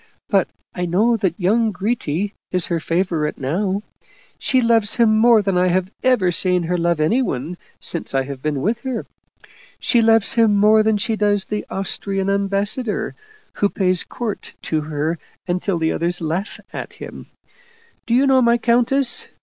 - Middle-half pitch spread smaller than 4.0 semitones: No, average, 4.6 semitones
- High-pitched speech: Yes, high, 195 Hz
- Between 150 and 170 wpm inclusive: Yes, average, 165 wpm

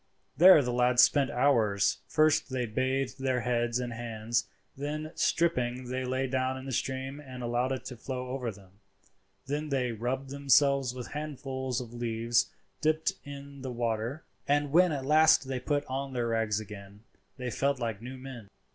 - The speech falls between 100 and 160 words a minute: No, average, 175 wpm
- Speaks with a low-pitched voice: Yes, low, 130 Hz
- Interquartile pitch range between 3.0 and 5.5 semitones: No, narrow, 2.6 semitones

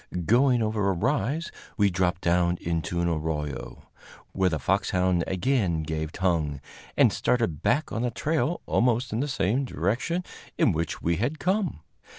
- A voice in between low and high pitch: No, very low, 95 Hz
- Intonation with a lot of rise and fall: Yes, wide, 6.7 semitones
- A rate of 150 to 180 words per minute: Yes, average, 160 wpm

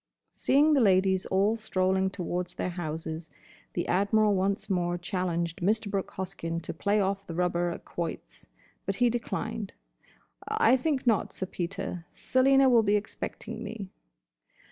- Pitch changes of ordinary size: Yes, average, 3.7 semitones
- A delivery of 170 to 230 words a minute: No, average, 145 wpm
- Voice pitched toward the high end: Yes, high, 195 Hz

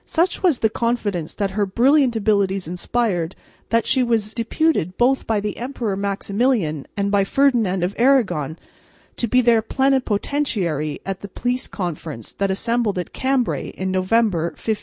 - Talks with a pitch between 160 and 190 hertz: No, high, 215 Hz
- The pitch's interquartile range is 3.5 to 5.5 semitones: Yes, average, 4.6 semitones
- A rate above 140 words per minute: Yes, average, 155 wpm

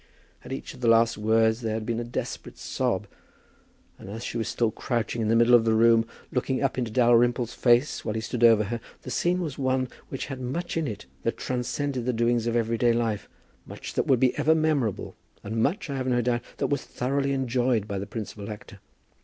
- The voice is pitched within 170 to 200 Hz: No, low, 120 Hz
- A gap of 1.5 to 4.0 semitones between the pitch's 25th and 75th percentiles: Yes, narrow, 2.5 semitones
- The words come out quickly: Yes, fast, 220 wpm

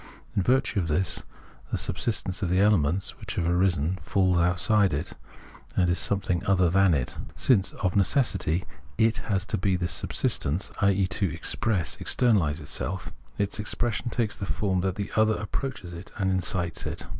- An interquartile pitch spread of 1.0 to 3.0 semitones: Yes, average, 2.7 semitones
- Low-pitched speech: Yes, very low, 95 Hz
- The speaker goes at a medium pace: Yes, average, 170 wpm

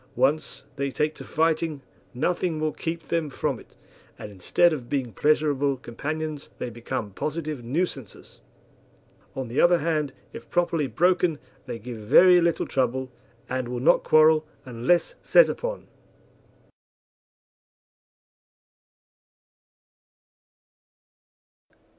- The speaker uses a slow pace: Yes, slow, 110 wpm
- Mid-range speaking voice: Yes, medium, 150 Hz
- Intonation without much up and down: No, average, 4.3 semitones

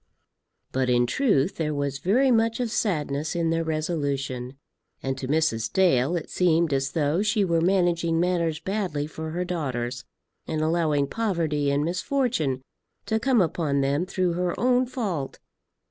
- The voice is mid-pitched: Yes, medium, 165 Hz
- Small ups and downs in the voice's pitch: No, average, 4.6 semitones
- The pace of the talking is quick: No, average, 155 wpm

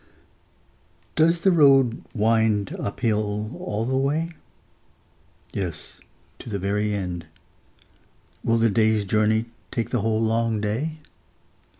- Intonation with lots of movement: No, average, 3.0 semitones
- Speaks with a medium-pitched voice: No, low, 110 Hz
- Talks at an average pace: No, slow, 115 wpm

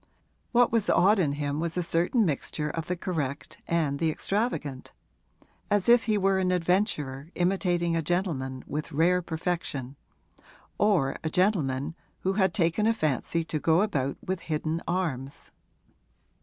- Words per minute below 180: Yes, average, 150 wpm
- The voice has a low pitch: No, medium, 170 Hz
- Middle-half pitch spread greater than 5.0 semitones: No, average, 4.2 semitones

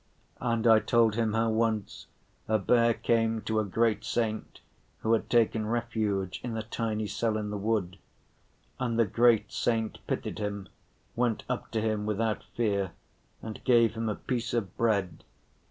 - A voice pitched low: Yes, low, 110 Hz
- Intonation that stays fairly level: Yes, narrow, 1.6 semitones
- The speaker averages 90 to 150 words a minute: No, average, 165 wpm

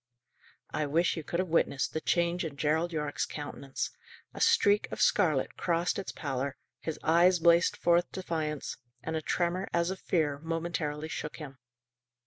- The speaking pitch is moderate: Yes, medium, 165 Hz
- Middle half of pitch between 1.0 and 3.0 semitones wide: Yes, narrow, 2.5 semitones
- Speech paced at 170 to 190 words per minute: No, average, 160 wpm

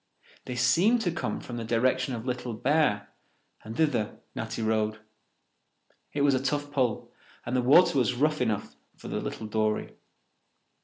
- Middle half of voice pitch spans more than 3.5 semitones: Yes, average, 4.4 semitones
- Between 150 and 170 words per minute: Yes, average, 160 wpm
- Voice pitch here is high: No, low, 125 Hz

